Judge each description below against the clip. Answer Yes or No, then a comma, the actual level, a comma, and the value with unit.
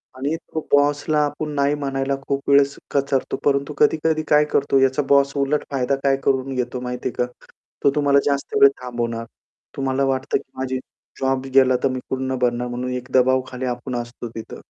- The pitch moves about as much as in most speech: No, narrow, 1.7 semitones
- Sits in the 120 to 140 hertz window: Yes, low, 135 Hz